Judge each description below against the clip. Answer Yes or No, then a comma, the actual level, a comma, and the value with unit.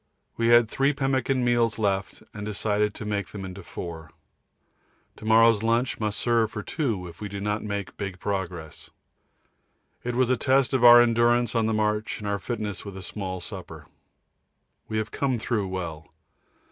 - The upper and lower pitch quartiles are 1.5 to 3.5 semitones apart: Yes, average, 3.0 semitones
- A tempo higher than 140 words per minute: Yes, average, 170 wpm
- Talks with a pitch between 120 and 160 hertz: No, low, 110 Hz